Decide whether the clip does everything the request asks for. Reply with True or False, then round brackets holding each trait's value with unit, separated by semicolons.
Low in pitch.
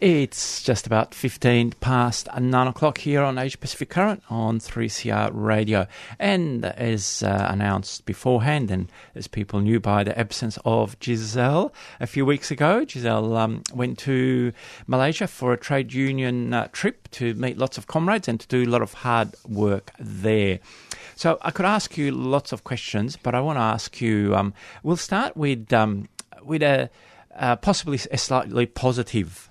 True (120 Hz)